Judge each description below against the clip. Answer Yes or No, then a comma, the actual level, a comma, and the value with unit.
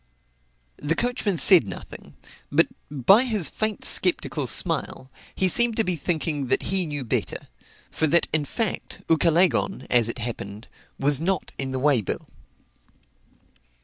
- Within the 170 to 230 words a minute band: No, average, 145 wpm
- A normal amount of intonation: No, wide, 6.0 semitones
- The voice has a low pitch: No, medium, 160 Hz